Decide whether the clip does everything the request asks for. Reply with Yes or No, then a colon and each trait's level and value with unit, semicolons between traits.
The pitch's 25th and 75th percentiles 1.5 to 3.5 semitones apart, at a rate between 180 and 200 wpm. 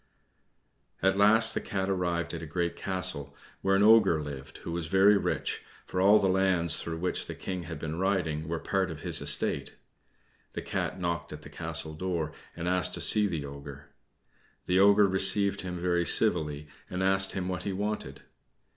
Yes: average, 3.2 semitones; average, 185 wpm